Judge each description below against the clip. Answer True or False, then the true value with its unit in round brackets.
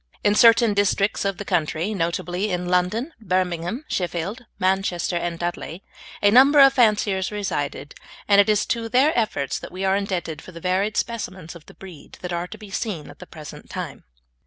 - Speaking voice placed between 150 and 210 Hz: True (190 Hz)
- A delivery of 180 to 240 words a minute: True (185 wpm)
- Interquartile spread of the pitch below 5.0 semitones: True (3.5 semitones)